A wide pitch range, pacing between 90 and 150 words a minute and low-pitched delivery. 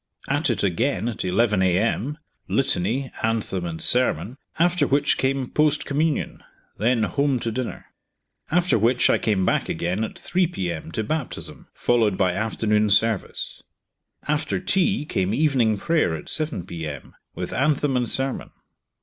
Yes: wide, 6.3 semitones; average, 145 wpm; low, 120 Hz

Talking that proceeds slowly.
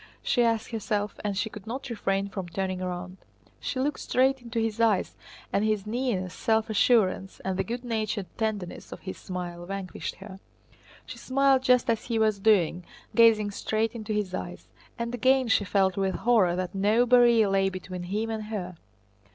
No: average, 180 wpm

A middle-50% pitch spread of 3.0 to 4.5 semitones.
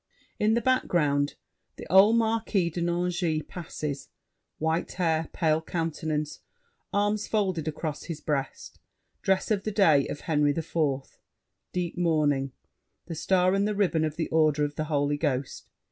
Yes: average, 3.9 semitones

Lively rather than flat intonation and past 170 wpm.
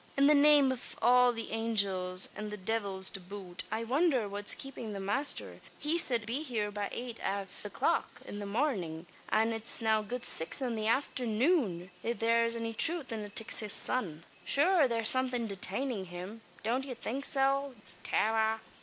No: average, 4.1 semitones; average, 185 wpm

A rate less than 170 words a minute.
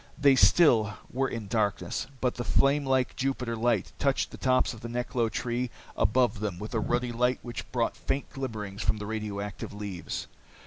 No: average, 180 wpm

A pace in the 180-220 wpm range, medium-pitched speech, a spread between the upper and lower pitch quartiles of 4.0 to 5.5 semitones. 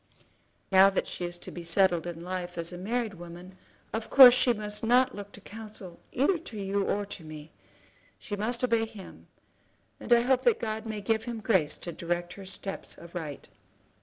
No: average, 195 wpm; high, 200 Hz; average, 4.3 semitones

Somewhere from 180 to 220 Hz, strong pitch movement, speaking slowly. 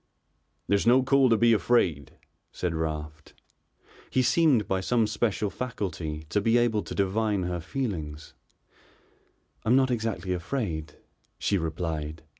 No: low, 100 Hz; wide, 6.5 semitones; slow, 130 wpm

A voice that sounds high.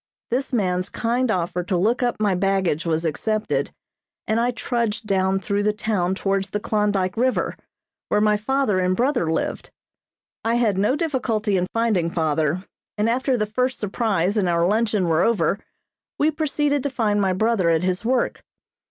Yes: high, 210 Hz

